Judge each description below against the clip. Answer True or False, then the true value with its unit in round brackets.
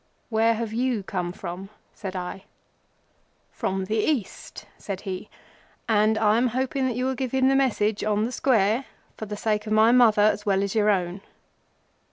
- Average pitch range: True (3.4 semitones)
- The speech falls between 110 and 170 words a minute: False (180 wpm)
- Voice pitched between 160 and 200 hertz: False (215 Hz)